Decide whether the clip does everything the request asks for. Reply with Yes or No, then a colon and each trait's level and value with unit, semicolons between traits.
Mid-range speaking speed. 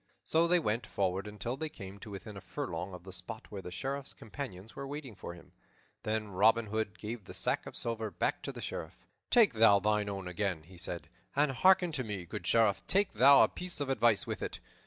No: fast, 220 wpm